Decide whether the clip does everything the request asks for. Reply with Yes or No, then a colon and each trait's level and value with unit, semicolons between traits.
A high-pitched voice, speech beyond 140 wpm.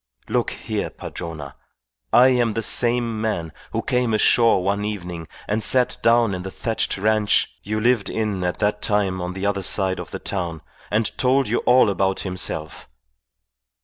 No: low, 105 Hz; average, 170 wpm